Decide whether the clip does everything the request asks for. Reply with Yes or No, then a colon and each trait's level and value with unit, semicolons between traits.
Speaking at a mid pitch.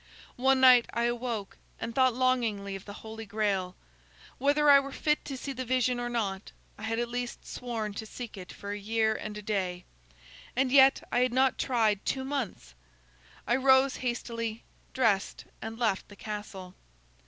No: high, 235 Hz